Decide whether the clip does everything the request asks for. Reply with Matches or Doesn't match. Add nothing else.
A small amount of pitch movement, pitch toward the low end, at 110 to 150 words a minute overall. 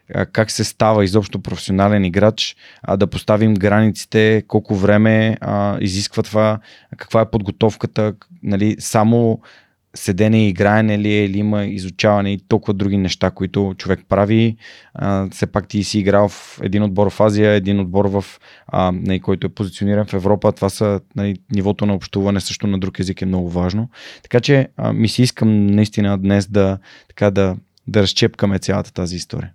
Doesn't match